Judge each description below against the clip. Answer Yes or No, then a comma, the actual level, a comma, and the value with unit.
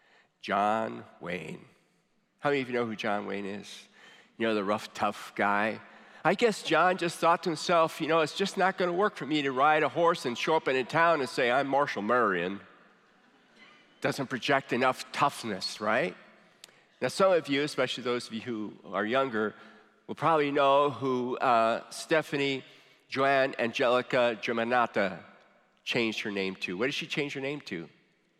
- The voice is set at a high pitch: No, low, 135 Hz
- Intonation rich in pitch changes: Yes, wide, 5.9 semitones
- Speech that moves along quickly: No, average, 180 wpm